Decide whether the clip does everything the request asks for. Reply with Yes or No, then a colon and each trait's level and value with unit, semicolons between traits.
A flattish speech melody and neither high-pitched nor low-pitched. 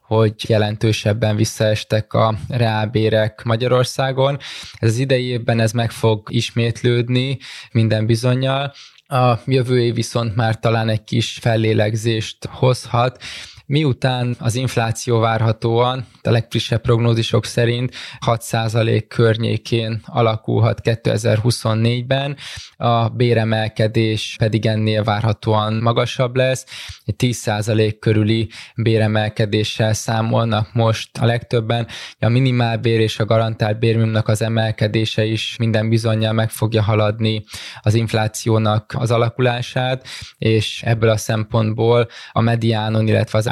No: narrow, 1.6 semitones; low, 115 Hz